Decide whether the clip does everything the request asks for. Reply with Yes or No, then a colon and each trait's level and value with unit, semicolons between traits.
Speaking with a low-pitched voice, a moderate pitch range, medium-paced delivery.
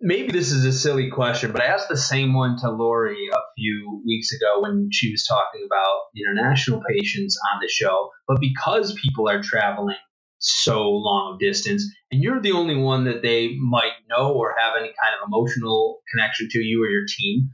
No: low, 130 Hz; wide, 8.2 semitones; average, 195 wpm